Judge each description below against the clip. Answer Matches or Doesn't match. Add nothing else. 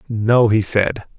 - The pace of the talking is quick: Doesn't match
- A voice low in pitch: Matches